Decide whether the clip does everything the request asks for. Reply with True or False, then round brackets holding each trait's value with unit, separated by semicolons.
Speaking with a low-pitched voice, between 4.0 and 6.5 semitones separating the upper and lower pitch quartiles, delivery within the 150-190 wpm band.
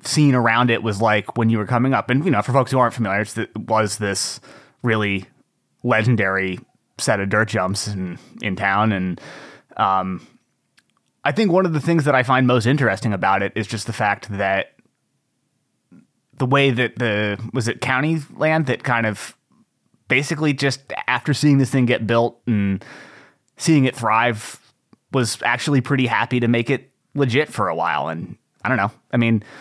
True (115 Hz; 4.3 semitones; 180 wpm)